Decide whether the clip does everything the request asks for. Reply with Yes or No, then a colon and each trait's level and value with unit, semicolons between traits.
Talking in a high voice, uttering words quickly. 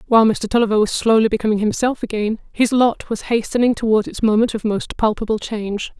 No: high, 220 Hz; average, 190 wpm